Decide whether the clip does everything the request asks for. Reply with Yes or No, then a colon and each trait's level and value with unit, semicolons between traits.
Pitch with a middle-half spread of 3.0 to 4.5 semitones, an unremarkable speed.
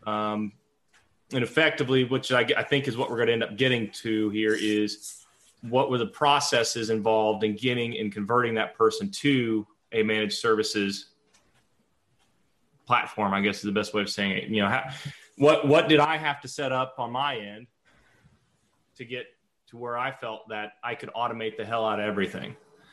Yes: average, 3.6 semitones; average, 190 wpm